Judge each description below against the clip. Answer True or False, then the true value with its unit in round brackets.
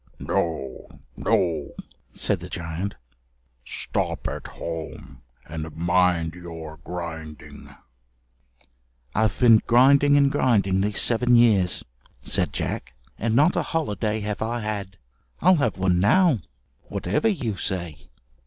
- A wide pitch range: True (6.1 semitones)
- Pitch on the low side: True (100 Hz)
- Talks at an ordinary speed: False (115 wpm)